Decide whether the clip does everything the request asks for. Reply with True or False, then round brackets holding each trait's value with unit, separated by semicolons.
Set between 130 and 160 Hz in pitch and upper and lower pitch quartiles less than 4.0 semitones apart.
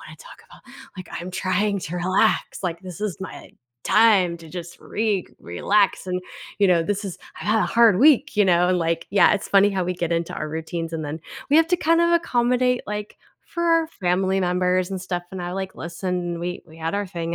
False (185 Hz; 3.2 semitones)